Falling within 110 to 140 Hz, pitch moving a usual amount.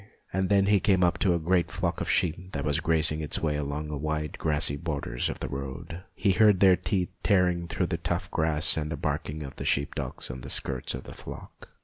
No: very low, 80 Hz; average, 3.6 semitones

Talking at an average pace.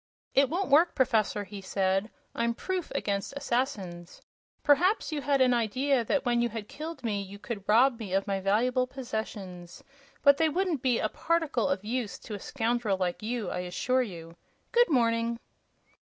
Yes: average, 175 wpm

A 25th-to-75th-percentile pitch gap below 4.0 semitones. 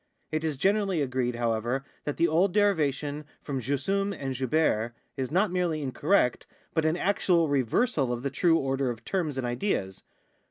No: average, 5.2 semitones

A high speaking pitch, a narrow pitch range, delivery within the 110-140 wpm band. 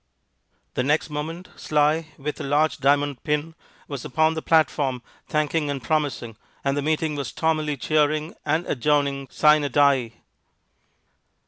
No: medium, 150 Hz; narrow, 1.8 semitones; slow, 135 wpm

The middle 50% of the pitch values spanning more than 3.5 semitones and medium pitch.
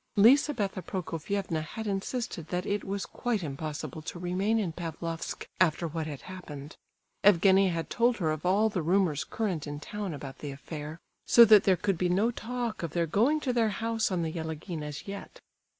Yes: average, 4.7 semitones; medium, 180 Hz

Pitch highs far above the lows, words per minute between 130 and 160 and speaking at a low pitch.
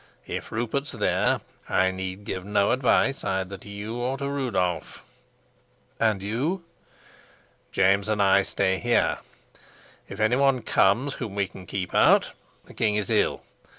No: average, 4.2 semitones; average, 150 wpm; low, 105 Hz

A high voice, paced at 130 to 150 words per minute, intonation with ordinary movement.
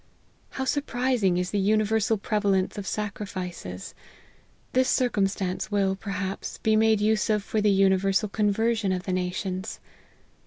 No: high, 205 Hz; average, 140 wpm; narrow, 2.3 semitones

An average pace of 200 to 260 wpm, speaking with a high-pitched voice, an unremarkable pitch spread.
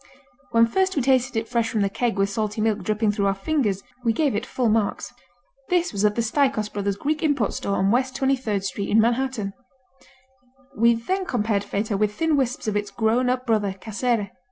Yes: fast, 205 wpm; high, 225 Hz; average, 3.8 semitones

